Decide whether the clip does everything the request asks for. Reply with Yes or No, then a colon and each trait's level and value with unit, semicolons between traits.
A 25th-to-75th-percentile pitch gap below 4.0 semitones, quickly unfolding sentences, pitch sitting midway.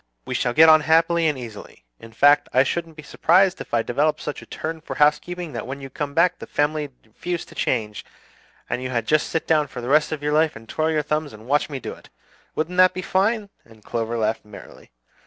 No: average, 4.5 semitones; fast, 235 wpm; medium, 150 Hz